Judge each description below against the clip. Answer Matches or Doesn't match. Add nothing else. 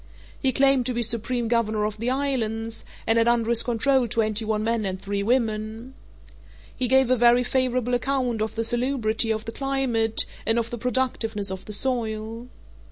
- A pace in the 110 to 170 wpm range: Doesn't match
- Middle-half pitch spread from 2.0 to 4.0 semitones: Matches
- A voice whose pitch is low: Doesn't match